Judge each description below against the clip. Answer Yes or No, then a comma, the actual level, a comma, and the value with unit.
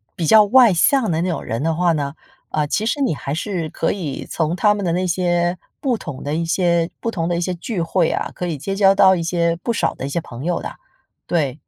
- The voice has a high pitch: No, medium, 175 Hz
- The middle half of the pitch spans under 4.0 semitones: Yes, average, 3.2 semitones